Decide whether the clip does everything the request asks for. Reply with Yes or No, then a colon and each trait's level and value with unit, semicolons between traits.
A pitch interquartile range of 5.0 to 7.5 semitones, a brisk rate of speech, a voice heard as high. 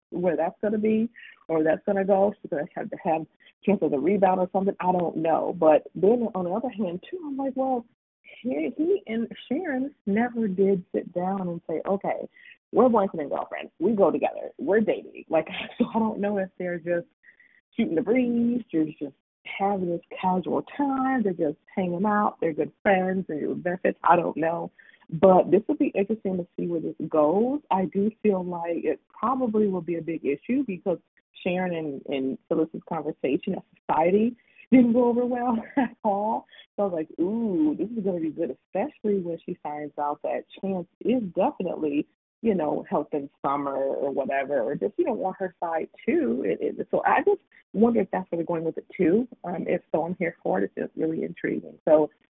Yes: wide, 5.6 semitones; fast, 210 wpm; high, 195 Hz